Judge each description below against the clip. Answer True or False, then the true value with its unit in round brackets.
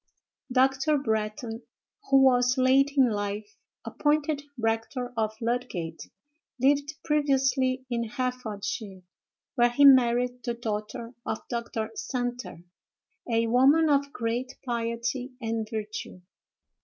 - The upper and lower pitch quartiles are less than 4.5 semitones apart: True (2.9 semitones)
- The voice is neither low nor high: False (245 Hz)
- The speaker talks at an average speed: False (105 wpm)